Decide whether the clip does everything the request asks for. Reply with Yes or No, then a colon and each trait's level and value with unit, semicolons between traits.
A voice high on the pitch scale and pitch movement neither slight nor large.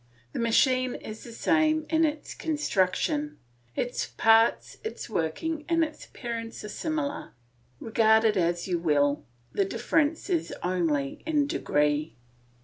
No: high, 230 Hz; wide, 8.9 semitones